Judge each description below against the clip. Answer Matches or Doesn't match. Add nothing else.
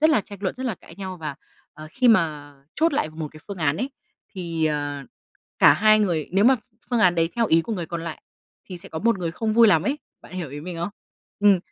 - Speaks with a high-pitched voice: Doesn't match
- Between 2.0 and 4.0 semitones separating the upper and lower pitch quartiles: Doesn't match